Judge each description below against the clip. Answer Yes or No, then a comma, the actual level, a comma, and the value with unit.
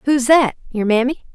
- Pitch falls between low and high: No, very high, 255 Hz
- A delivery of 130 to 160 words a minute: Yes, slow, 135 wpm